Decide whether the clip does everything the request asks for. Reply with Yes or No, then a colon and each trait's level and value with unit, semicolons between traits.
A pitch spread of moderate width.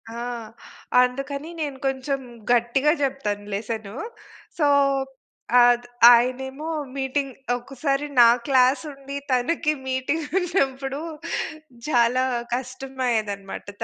No: narrow, 2.3 semitones